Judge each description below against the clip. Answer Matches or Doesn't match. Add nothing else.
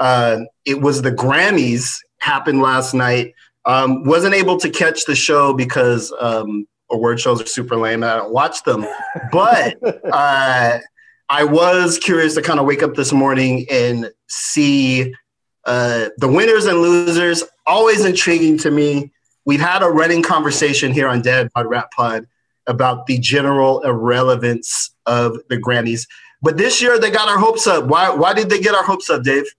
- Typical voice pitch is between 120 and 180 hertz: Matches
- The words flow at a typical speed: Matches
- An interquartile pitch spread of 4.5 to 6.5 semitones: Matches